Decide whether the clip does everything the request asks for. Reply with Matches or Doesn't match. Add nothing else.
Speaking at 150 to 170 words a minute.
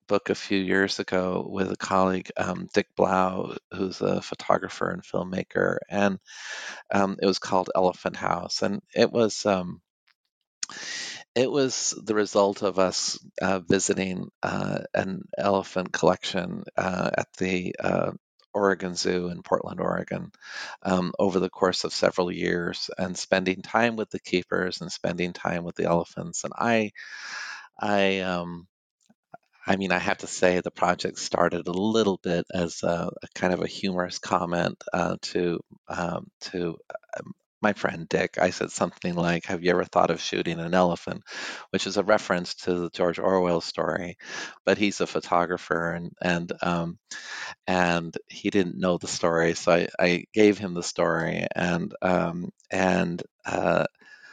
Matches